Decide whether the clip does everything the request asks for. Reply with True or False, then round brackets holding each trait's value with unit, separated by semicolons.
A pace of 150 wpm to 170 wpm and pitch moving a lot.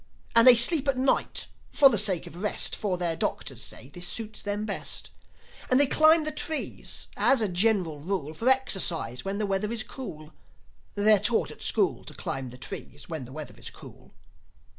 False (190 wpm; 7.0 semitones)